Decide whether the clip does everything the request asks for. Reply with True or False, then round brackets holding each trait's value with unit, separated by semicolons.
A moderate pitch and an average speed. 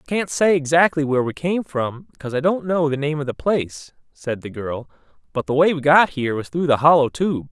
False (145 Hz; 250 wpm)